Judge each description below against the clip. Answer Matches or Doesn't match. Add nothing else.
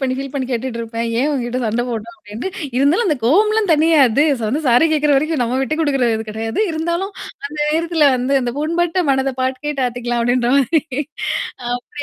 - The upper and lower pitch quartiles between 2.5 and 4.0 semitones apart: Doesn't match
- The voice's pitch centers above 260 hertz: Matches